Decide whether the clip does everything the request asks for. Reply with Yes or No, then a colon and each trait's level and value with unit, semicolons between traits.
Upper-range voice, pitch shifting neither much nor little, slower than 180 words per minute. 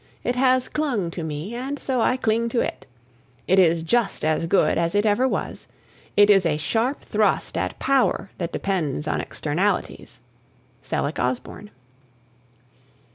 No: high, 200 Hz; wide, 6.7 semitones; average, 150 wpm